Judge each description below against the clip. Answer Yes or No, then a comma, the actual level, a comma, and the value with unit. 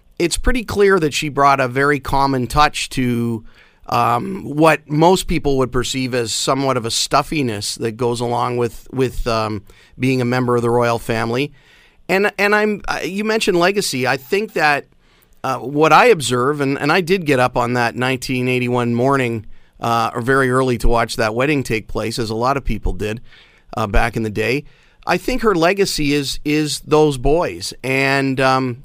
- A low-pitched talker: Yes, low, 130 Hz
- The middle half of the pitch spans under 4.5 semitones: Yes, average, 3.9 semitones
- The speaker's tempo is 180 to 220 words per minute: Yes, average, 185 wpm